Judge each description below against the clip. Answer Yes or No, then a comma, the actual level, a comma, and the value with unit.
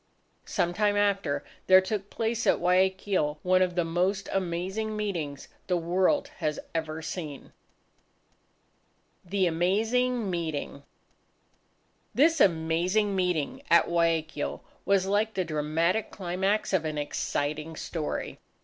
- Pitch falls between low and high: Yes, medium, 180 Hz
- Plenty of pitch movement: No, average, 3.7 semitones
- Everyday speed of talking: No, slow, 115 wpm